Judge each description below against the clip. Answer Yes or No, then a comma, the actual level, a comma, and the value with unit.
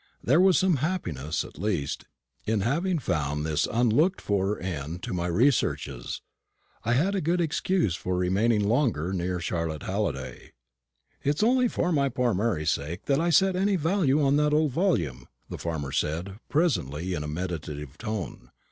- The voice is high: No, low, 105 Hz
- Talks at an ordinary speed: Yes, average, 160 wpm